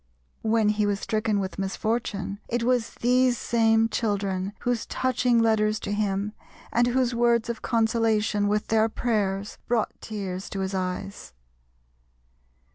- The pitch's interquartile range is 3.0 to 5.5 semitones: No, narrow, 2.5 semitones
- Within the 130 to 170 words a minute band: Yes, slow, 135 wpm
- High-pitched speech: Yes, high, 220 Hz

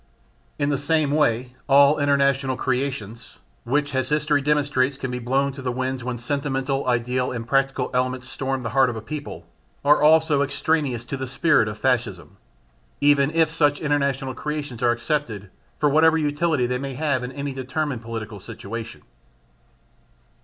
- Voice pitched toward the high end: No, low, 135 Hz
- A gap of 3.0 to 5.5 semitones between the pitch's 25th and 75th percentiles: No, narrow, 2.6 semitones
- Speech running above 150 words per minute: Yes, average, 160 wpm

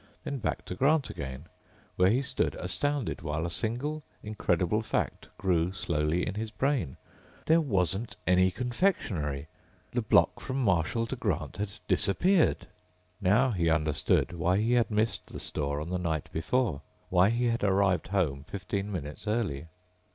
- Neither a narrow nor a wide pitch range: No, wide, 6.1 semitones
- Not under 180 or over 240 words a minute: No, average, 155 wpm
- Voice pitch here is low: Yes, very low, 95 Hz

